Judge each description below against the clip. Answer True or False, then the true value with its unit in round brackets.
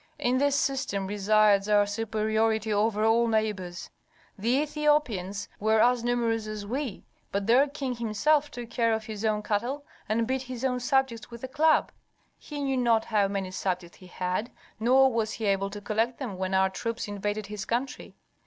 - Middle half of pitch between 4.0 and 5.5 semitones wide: False (3.4 semitones)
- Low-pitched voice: False (220 Hz)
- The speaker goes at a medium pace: True (180 wpm)